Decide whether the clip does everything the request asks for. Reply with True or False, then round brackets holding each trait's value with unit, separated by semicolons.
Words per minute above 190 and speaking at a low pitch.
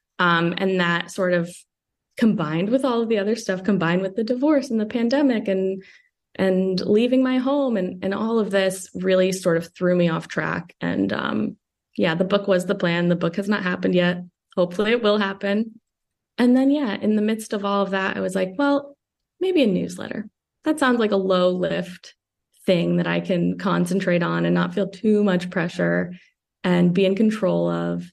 False (200 wpm; 190 Hz)